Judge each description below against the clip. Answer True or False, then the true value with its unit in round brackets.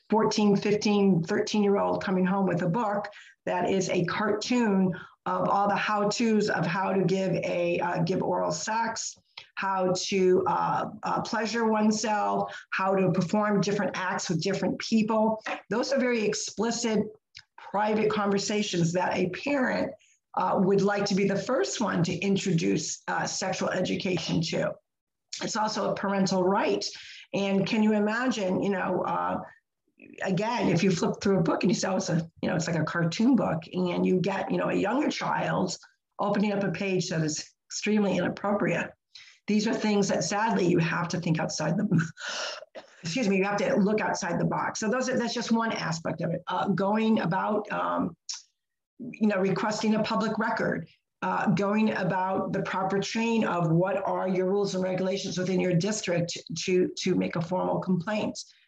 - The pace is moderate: True (180 wpm)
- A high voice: True (195 Hz)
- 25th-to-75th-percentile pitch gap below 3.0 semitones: True (2.6 semitones)